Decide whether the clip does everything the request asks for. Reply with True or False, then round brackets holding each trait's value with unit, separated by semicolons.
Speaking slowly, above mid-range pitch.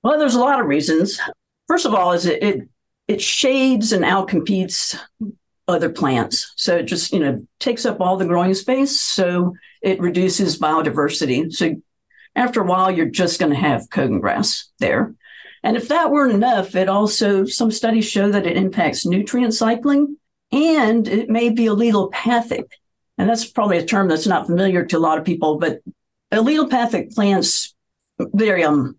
False (170 wpm; 205 Hz)